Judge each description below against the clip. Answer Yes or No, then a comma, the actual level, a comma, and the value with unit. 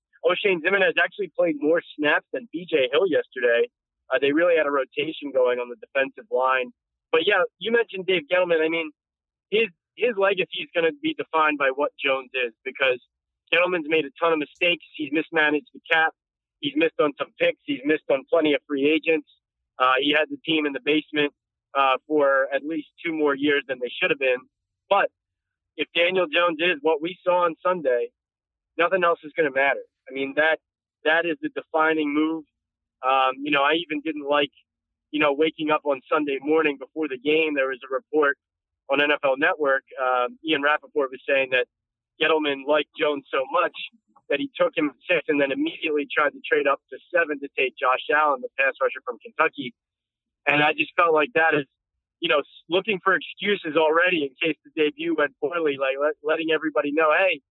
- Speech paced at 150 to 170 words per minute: No, average, 200 wpm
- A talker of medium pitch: Yes, medium, 155 Hz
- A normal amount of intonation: Yes, average, 4.4 semitones